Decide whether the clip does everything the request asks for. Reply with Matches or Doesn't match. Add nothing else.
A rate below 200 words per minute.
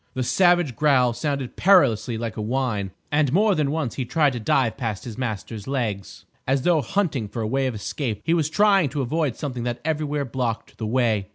Doesn't match